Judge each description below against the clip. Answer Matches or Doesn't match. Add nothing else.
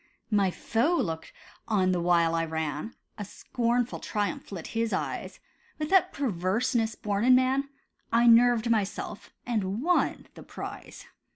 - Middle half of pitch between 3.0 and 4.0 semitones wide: Doesn't match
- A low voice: Doesn't match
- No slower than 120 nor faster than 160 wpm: Matches